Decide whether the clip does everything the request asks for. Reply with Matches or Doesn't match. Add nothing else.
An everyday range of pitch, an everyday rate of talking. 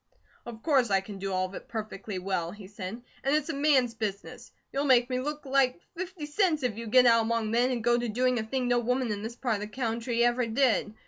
Doesn't match